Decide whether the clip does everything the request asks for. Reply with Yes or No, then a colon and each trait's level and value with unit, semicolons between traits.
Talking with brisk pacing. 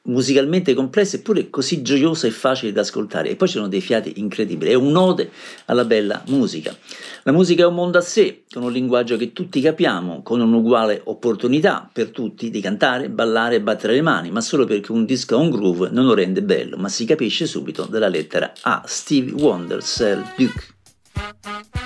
Yes: fast, 190 wpm